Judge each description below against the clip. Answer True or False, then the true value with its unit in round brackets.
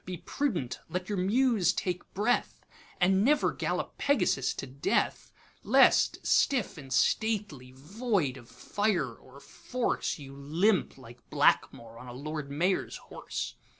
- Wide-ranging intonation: True (7.6 semitones)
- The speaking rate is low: True (120 wpm)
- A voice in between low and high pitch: True (175 Hz)